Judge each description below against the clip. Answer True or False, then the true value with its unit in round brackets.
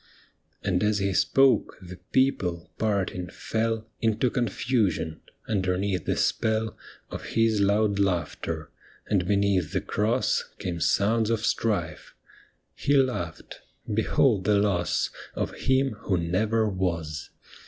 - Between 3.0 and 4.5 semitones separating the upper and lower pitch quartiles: True (3.7 semitones)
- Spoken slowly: True (120 wpm)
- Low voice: True (100 Hz)